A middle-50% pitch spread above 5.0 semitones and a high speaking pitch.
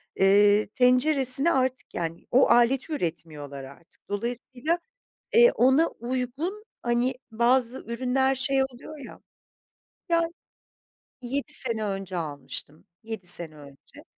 Yes: wide, 5.6 semitones; high, 240 Hz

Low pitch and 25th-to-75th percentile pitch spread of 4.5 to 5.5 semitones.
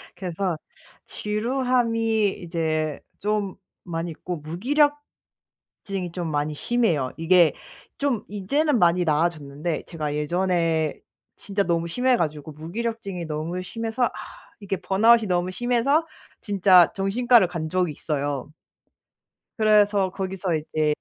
No: medium, 185 Hz; average, 5.2 semitones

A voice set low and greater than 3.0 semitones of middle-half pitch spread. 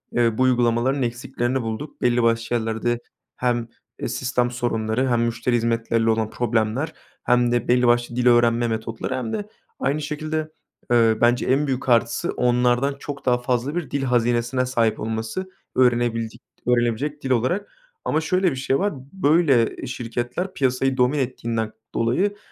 No: low, 120 Hz; narrow, 2.4 semitones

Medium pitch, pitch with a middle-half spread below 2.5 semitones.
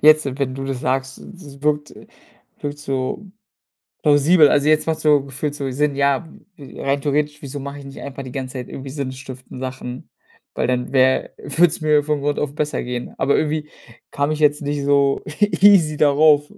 Yes: medium, 145 Hz; narrow, 1.8 semitones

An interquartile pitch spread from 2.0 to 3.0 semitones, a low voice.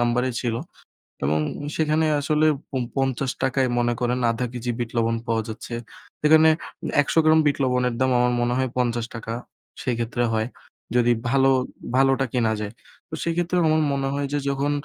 Yes: narrow, 2.6 semitones; low, 125 Hz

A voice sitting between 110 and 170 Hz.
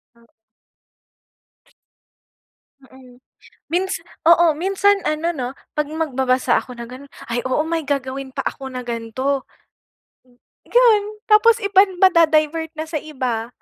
No: very high, 300 Hz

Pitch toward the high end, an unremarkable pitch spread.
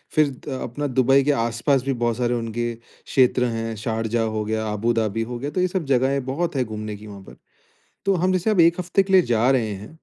No: low, 120 Hz; average, 4.3 semitones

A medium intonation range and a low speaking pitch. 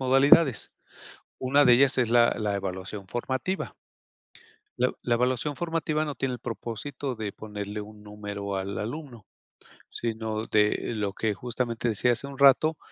Yes: average, 4.2 semitones; low, 120 Hz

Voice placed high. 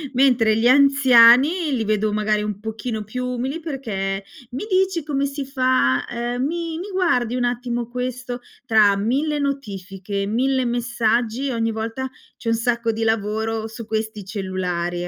Yes: high, 235 Hz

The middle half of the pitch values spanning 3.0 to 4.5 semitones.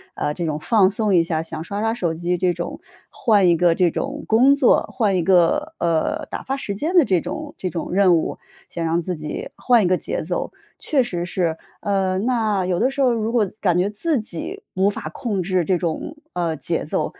No: average, 5.1 semitones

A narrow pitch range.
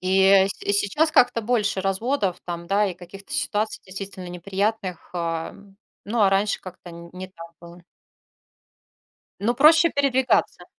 No: average, 3.7 semitones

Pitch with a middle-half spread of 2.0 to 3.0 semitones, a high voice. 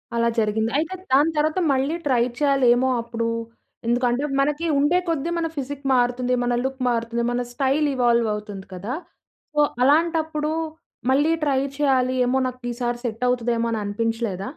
No: average, 3.6 semitones; very high, 250 Hz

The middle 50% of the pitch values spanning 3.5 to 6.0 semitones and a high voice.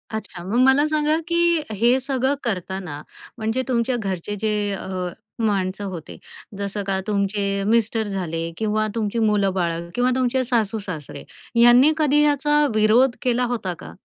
Yes: average, 4.7 semitones; high, 220 Hz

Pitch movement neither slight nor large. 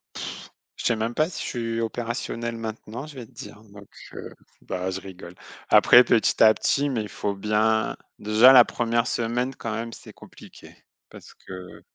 No: narrow, 2.1 semitones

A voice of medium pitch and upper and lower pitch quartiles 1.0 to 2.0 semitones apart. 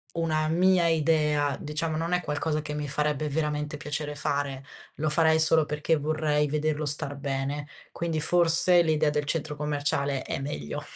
Yes: medium, 150 Hz; narrow, 1.5 semitones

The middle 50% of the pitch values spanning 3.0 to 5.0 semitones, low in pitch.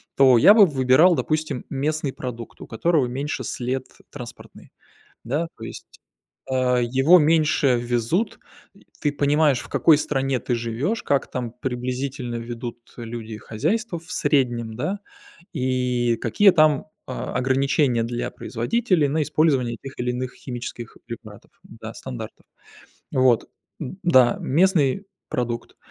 Yes: average, 4.1 semitones; low, 130 Hz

